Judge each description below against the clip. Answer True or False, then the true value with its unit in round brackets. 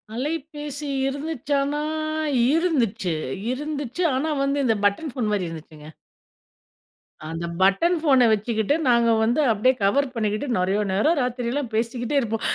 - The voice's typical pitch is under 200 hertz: False (245 Hz)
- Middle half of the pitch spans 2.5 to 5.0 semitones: False (5.4 semitones)